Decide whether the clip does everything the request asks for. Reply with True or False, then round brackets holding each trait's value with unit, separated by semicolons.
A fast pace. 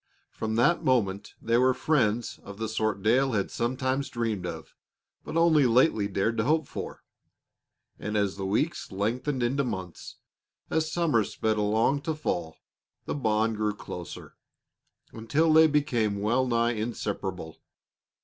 False (145 wpm)